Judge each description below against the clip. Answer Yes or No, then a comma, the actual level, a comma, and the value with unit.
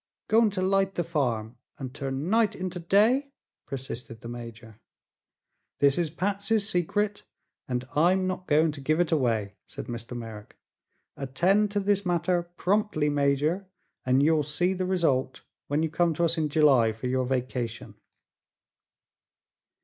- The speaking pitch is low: No, medium, 155 Hz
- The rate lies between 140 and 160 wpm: Yes, average, 150 wpm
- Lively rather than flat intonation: Yes, wide, 6.3 semitones